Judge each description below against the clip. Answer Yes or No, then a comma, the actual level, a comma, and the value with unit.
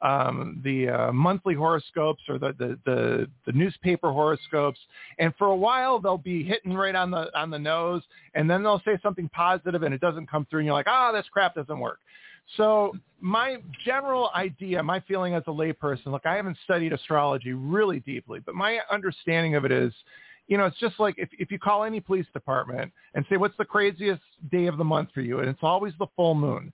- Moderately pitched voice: Yes, medium, 175 Hz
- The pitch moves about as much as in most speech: Yes, average, 5.0 semitones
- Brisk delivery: Yes, fast, 215 wpm